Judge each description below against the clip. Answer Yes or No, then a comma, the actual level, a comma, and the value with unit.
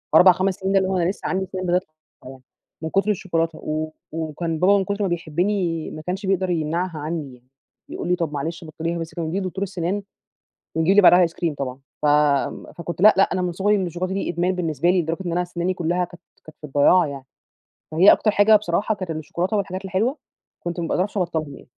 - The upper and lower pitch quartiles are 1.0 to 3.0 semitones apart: Yes, average, 2.7 semitones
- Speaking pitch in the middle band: Yes, medium, 175 Hz